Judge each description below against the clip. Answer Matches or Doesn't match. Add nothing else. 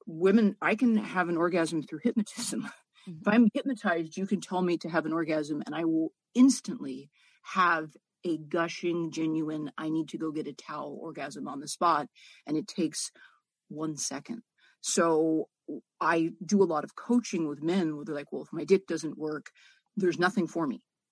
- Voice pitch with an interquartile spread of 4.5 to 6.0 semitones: Matches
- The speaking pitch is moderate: Matches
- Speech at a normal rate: Matches